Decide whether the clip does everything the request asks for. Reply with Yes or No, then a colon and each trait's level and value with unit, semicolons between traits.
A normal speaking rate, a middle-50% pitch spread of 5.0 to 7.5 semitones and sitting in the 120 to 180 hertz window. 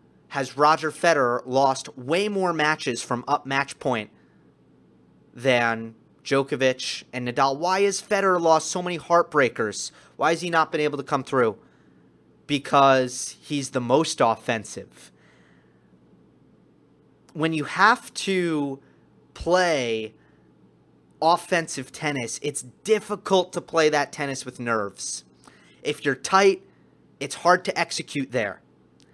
No: slow, 120 wpm; wide, 5.4 semitones; medium, 140 Hz